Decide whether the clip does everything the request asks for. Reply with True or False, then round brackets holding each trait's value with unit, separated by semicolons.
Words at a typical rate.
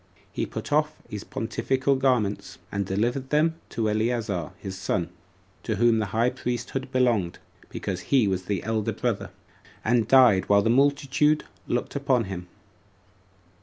True (145 wpm)